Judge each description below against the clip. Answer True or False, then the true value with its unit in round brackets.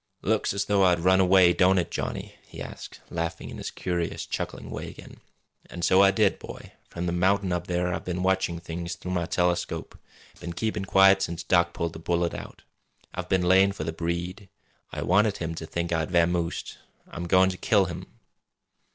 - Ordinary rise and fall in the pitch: False (1.7 semitones)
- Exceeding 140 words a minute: True (195 wpm)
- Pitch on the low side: True (90 Hz)